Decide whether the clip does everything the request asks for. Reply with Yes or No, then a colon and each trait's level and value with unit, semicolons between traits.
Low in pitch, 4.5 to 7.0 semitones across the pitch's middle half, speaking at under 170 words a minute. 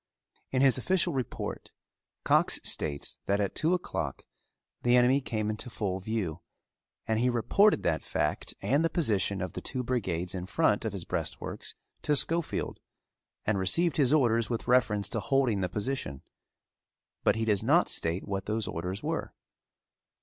Yes: low, 110 Hz; wide, 5.4 semitones; average, 160 wpm